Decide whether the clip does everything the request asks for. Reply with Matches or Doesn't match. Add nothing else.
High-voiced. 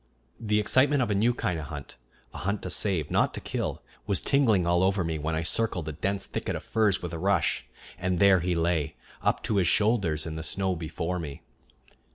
Doesn't match